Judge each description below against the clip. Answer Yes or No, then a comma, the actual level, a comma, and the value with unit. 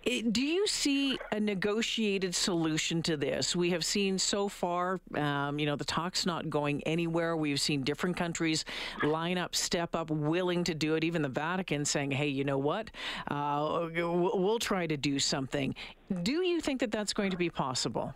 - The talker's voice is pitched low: No, medium, 170 Hz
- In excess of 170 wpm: Yes, average, 185 wpm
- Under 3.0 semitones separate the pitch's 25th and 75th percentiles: No, average, 4.8 semitones